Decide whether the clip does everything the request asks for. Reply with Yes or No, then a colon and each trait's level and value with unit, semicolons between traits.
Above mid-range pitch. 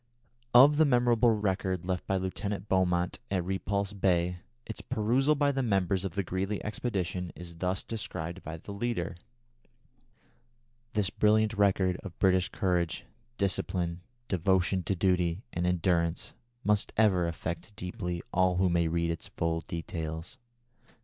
No: very low, 95 Hz